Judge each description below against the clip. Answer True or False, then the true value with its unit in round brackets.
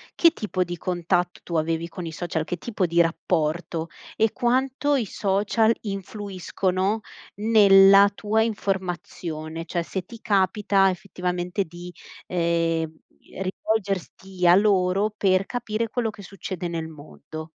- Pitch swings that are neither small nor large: True (3.2 semitones)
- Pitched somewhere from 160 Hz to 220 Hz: True (185 Hz)